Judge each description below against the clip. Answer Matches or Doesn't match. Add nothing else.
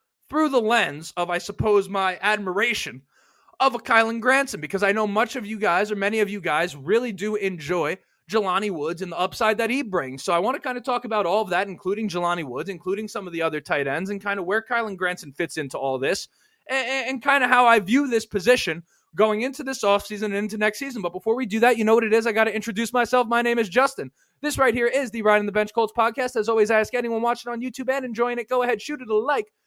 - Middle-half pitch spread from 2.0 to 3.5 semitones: Doesn't match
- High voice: Matches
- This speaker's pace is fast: Matches